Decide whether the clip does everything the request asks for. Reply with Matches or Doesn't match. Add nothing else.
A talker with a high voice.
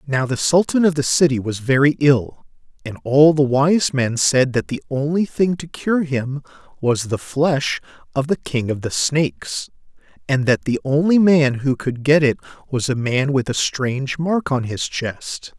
Doesn't match